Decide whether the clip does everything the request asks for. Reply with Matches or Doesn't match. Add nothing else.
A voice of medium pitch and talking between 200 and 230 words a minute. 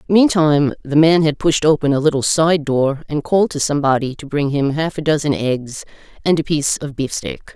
Matches